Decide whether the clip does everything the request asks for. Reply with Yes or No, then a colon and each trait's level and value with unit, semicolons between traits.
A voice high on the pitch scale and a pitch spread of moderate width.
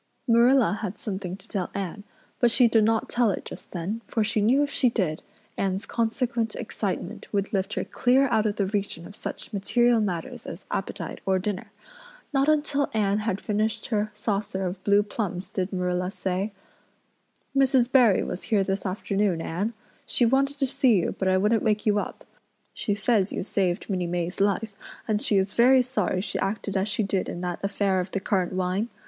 Yes: high, 205 Hz; average, 3.3 semitones